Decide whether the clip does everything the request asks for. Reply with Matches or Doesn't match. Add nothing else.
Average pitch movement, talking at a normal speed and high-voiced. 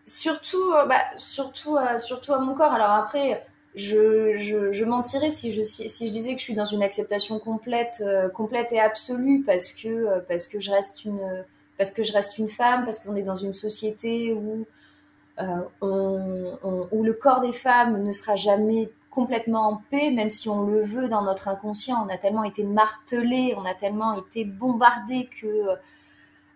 Matches